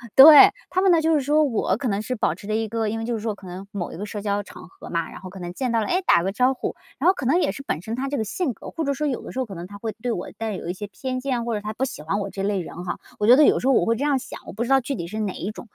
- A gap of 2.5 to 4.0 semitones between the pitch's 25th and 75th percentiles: No, average, 5.0 semitones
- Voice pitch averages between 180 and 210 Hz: No, high, 225 Hz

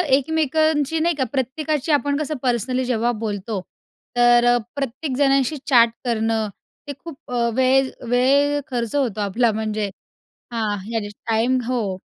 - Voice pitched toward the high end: Yes, very high, 255 Hz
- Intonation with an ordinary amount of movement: Yes, average, 3.7 semitones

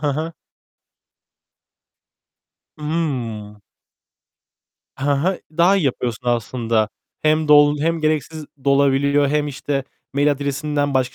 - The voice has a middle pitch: Yes, medium, 145 Hz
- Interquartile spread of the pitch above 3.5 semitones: No, narrow, 2.5 semitones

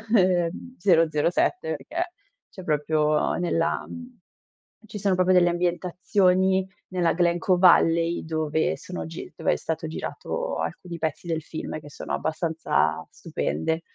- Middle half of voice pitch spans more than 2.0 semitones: Yes, narrow, 2.5 semitones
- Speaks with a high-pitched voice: No, medium, 170 Hz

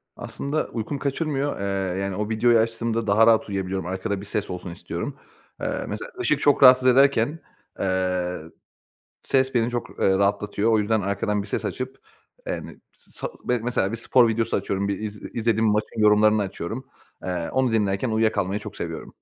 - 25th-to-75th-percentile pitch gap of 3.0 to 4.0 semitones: Yes, average, 3.5 semitones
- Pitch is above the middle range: No, low, 110 Hz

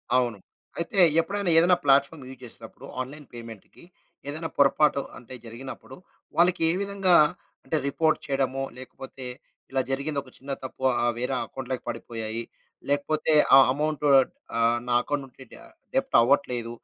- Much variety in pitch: No, average, 3.6 semitones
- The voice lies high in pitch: No, low, 135 Hz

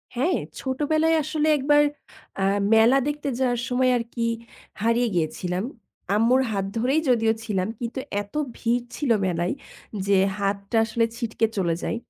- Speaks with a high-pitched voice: Yes, high, 235 Hz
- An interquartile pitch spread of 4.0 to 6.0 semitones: Yes, average, 4.7 semitones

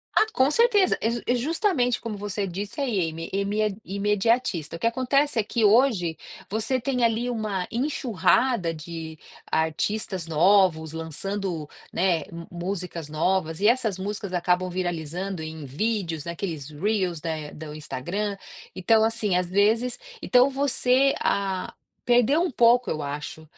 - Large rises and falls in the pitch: Yes, wide, 5.8 semitones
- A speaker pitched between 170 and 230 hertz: Yes, high, 200 Hz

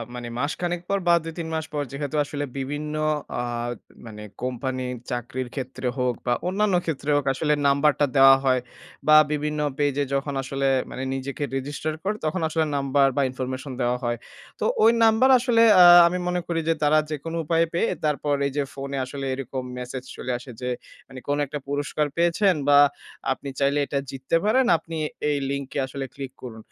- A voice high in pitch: No, medium, 140 Hz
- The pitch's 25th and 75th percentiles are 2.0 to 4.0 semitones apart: Yes, average, 3.1 semitones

